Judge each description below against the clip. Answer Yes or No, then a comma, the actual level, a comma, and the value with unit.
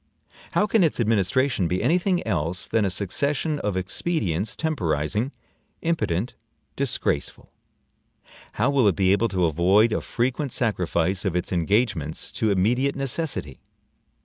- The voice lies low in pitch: Yes, low, 105 Hz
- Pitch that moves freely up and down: Yes, wide, 7.1 semitones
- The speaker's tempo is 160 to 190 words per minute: No, slow, 135 wpm